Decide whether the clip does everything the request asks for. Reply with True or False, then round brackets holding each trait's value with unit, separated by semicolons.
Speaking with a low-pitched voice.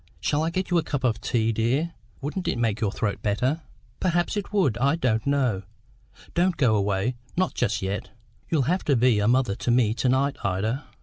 True (125 Hz)